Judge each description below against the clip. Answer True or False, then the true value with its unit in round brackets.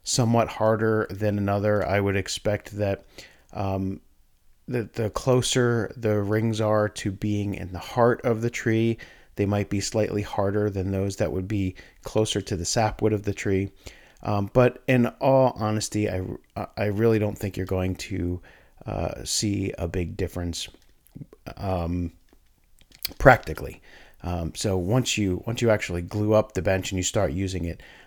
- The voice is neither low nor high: False (100 Hz)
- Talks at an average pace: True (165 wpm)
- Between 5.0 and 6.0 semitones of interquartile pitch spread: False (2.6 semitones)